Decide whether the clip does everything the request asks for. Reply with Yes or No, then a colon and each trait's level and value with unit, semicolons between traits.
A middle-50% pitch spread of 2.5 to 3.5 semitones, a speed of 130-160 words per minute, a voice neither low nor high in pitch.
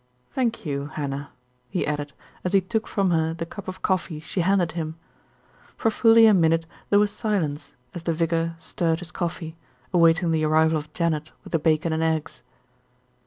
No: average, 2.8 semitones; average, 180 wpm; medium, 165 Hz